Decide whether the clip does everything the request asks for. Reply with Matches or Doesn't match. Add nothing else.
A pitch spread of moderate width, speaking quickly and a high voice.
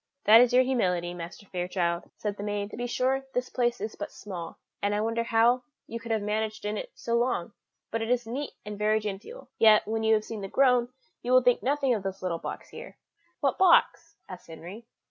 Matches